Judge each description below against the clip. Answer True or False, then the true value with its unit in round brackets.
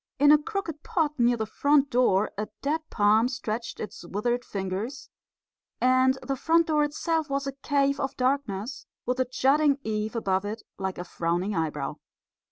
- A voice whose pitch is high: True (255 Hz)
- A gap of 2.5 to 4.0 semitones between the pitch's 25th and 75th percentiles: False (5.2 semitones)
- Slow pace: False (170 wpm)